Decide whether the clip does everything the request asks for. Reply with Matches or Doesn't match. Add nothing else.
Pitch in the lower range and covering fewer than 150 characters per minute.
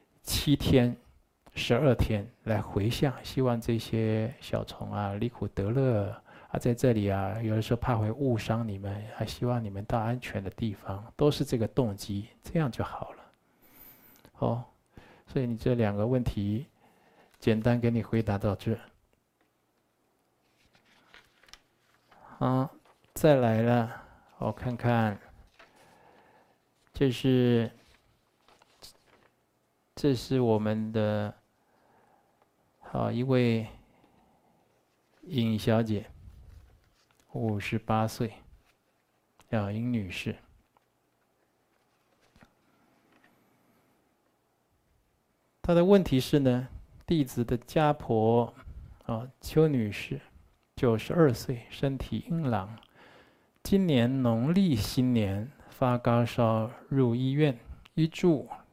Matches